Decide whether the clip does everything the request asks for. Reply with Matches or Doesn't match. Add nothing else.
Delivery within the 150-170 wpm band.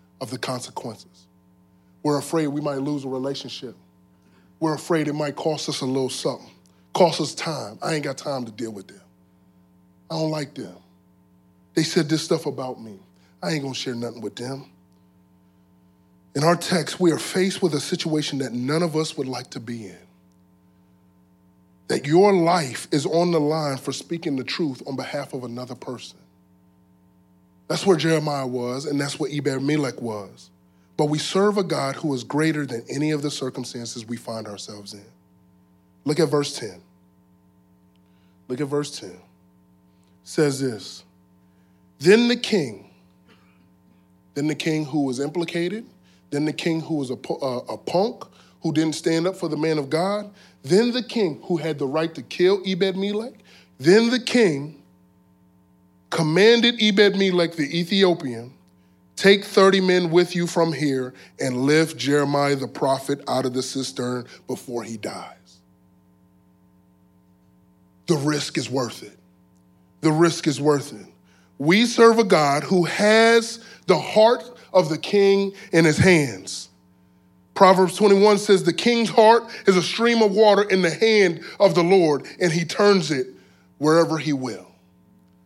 Matches